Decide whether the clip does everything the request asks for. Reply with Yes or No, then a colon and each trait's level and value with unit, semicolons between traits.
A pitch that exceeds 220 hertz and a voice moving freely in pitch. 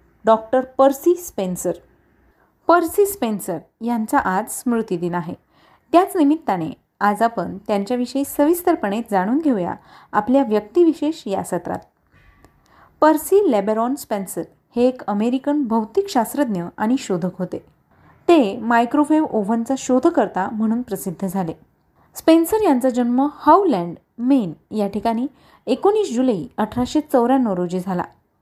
Yes: high, 245 Hz; wide, 6.2 semitones